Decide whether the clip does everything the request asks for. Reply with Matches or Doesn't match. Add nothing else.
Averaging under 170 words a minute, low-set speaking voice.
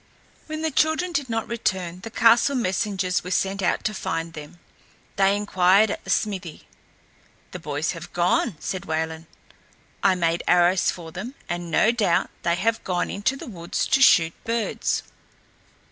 Doesn't match